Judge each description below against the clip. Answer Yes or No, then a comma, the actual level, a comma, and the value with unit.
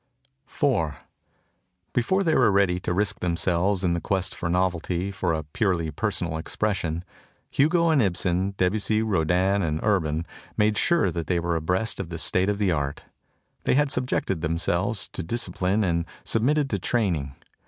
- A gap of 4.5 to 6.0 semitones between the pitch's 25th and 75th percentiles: No, average, 4.0 semitones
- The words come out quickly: No, average, 165 wpm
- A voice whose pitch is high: No, very low, 95 Hz